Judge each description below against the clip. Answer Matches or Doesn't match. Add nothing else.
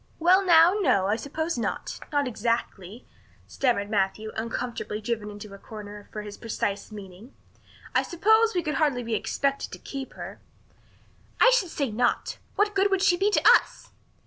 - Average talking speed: Matches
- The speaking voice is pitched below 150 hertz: Doesn't match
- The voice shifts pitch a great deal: Matches